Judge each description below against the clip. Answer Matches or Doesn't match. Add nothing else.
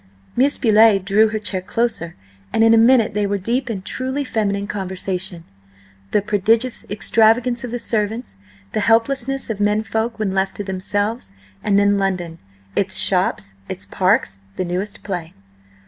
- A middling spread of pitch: Matches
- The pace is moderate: Matches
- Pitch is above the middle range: Matches